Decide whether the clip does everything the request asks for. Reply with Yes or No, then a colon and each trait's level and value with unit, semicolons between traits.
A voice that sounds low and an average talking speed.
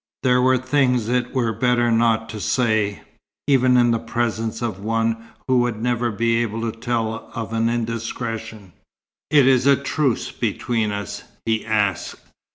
Yes: low, 115 Hz; average, 160 wpm